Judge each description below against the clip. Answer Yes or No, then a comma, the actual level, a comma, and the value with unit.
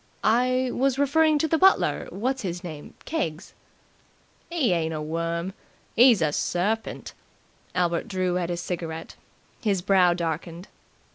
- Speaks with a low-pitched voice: No, medium, 185 Hz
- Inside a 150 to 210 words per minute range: No, slow, 135 wpm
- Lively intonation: Yes, wide, 7.0 semitones